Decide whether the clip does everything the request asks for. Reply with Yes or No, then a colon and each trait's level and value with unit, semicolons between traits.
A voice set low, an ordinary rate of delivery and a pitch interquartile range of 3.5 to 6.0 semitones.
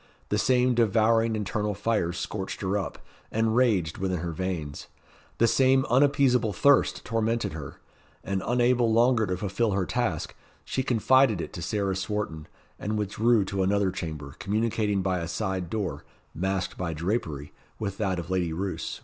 Yes: low, 100 Hz; average, 160 wpm; average, 3.8 semitones